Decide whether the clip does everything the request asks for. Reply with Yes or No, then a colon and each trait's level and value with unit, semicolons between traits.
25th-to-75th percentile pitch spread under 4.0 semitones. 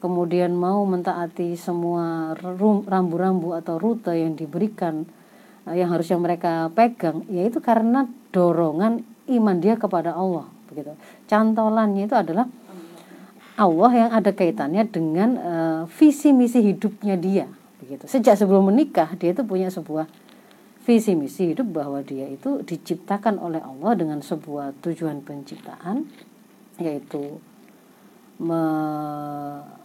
No: average, 4.8 semitones